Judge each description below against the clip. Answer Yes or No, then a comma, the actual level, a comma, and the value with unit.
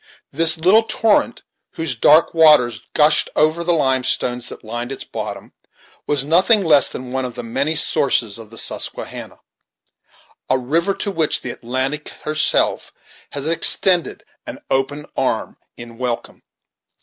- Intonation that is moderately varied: Yes, average, 4.7 semitones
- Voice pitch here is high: No, medium, 145 Hz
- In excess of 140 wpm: No, slow, 135 wpm